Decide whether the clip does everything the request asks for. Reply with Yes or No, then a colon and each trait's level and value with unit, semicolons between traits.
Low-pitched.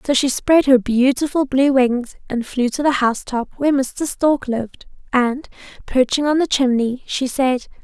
No: very high, 265 Hz